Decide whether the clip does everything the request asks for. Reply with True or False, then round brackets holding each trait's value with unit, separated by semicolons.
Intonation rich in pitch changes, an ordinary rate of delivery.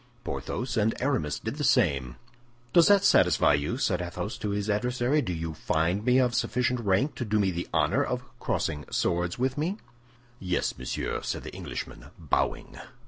True (6.4 semitones; 175 wpm)